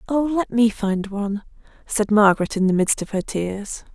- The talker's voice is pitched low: No, high, 210 Hz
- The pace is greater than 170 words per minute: Yes, average, 200 wpm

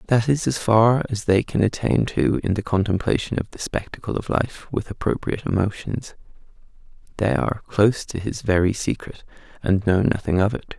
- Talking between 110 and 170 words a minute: No, average, 180 wpm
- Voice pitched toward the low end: Yes, low, 105 Hz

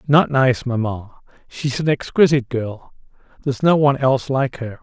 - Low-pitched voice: Yes, low, 130 Hz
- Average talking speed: Yes, average, 160 wpm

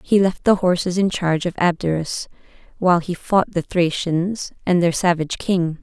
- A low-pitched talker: No, medium, 175 Hz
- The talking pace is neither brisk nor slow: Yes, average, 175 wpm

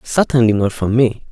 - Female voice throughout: No, male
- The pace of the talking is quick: No, average, 180 wpm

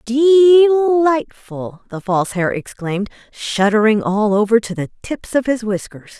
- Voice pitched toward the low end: No, high, 230 Hz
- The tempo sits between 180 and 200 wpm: No, average, 145 wpm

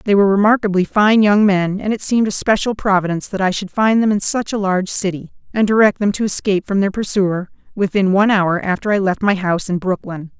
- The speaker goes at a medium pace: No, fast, 230 wpm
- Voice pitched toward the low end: No, high, 200 Hz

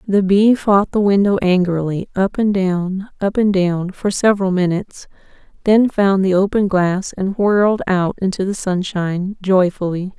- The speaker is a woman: Yes, female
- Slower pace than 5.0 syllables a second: Yes, 4.5 syllables/s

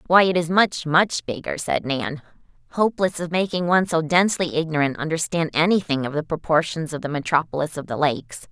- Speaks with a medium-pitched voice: Yes, medium, 160 Hz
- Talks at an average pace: Yes, average, 185 wpm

